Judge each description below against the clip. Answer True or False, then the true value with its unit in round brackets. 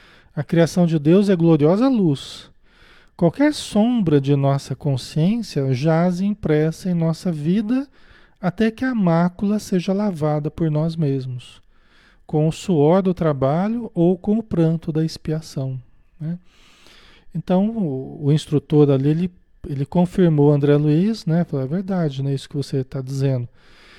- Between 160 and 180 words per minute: False (145 wpm)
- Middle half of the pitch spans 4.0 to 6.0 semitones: True (4.3 semitones)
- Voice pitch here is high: False (165 Hz)